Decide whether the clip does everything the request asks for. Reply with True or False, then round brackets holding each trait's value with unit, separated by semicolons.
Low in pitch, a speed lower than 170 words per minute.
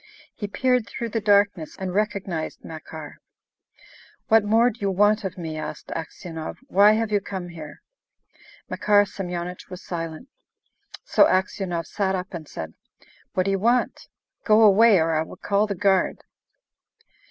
False (195 Hz; 155 wpm)